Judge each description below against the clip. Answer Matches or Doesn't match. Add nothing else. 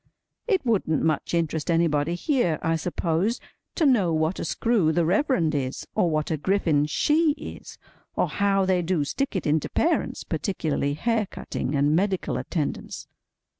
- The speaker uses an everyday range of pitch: Matches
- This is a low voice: Doesn't match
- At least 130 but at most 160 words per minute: Matches